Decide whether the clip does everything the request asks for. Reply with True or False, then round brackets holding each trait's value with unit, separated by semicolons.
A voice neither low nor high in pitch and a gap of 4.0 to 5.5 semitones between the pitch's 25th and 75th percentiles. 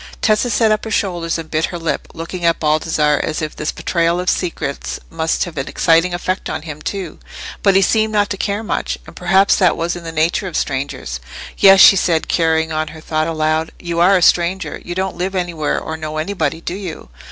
False (170 Hz; 3.1 semitones)